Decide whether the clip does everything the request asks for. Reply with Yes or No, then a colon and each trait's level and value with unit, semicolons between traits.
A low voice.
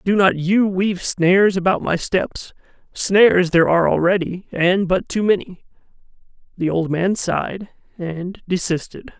No: medium, 185 Hz